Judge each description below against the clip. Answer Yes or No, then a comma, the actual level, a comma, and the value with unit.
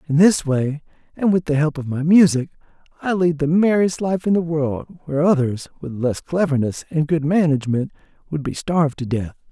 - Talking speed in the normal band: Yes, average, 195 wpm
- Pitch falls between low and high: Yes, medium, 155 Hz